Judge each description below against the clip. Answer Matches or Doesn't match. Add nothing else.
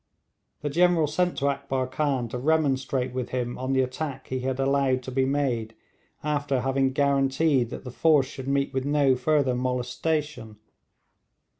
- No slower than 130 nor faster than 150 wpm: Doesn't match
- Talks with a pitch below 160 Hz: Matches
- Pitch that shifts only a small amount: Matches